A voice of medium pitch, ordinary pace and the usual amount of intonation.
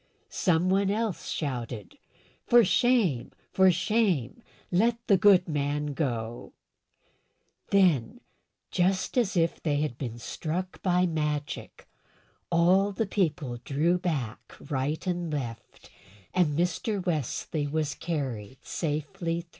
No: medium, 165 Hz; slow, 115 wpm; average, 4.5 semitones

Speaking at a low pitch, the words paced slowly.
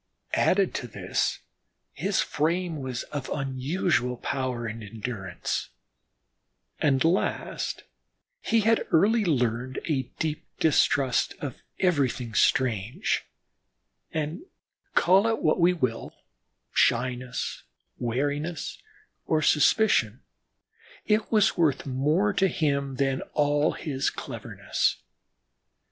No: medium, 145 Hz; slow, 100 wpm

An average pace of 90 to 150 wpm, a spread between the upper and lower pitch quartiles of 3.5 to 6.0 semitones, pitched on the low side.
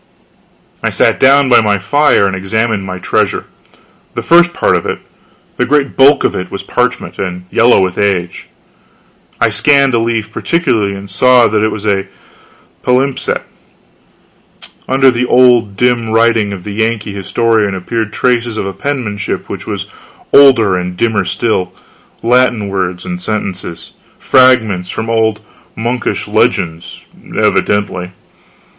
Yes: average, 140 wpm; average, 4.2 semitones; low, 110 Hz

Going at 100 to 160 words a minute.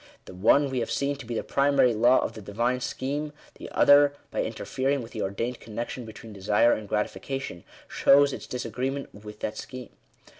No: average, 190 wpm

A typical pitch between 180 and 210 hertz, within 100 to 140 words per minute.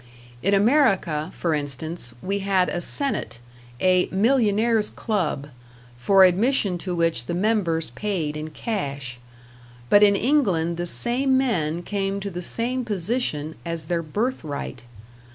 Yes: medium, 185 Hz; slow, 135 wpm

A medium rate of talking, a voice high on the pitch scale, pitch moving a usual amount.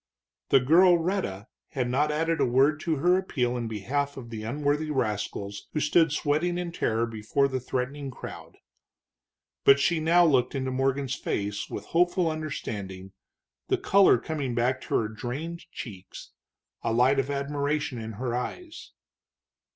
No: average, 155 wpm; low, 135 Hz; average, 4.7 semitones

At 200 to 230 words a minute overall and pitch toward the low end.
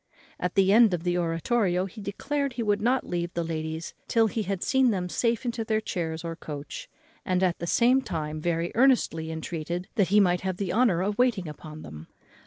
No: fast, 205 wpm; medium, 185 Hz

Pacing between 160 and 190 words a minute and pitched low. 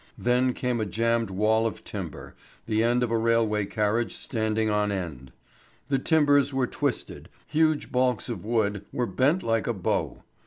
Yes: average, 165 wpm; low, 115 Hz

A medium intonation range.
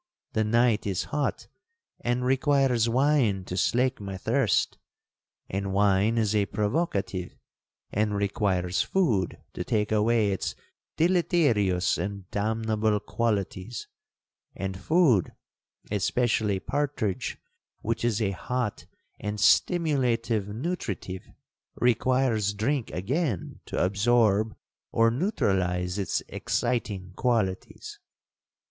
Yes: average, 4.0 semitones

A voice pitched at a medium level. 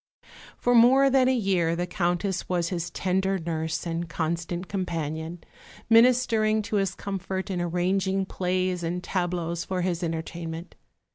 Yes: medium, 180 Hz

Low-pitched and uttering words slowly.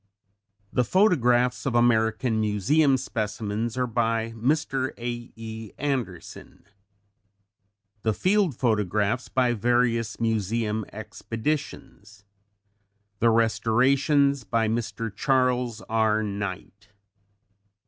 Yes: low, 115 Hz; slow, 85 wpm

